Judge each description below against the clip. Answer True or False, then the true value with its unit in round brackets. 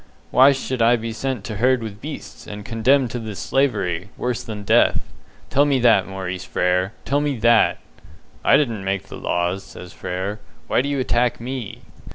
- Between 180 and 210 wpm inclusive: True (185 wpm)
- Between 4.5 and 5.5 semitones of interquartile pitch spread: True (4.9 semitones)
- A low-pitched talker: True (115 Hz)